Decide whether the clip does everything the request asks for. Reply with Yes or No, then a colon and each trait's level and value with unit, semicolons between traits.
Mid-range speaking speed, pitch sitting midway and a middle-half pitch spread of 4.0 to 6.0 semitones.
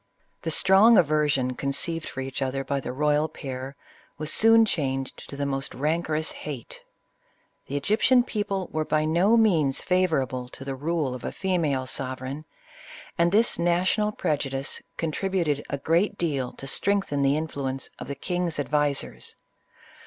Yes: average, 155 wpm; medium, 150 Hz; average, 4.5 semitones